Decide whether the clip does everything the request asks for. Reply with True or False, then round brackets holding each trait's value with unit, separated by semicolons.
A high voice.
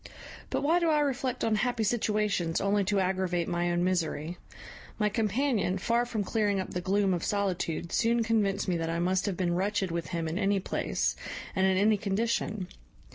True (195 Hz)